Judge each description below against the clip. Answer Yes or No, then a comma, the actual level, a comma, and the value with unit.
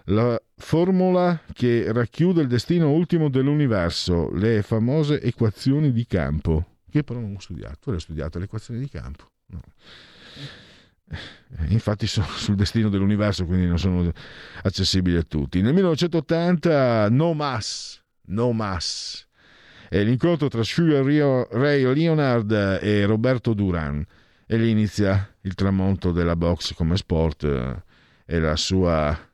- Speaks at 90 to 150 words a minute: Yes, average, 130 wpm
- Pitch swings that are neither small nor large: No, wide, 6.4 semitones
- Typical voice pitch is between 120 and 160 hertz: No, low, 105 Hz